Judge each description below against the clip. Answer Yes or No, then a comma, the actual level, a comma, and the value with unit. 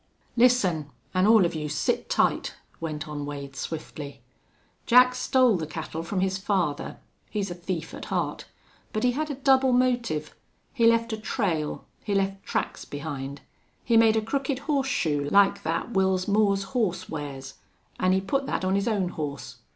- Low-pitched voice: No, high, 190 Hz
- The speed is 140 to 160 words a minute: No, average, 170 wpm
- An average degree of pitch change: No, wide, 6.9 semitones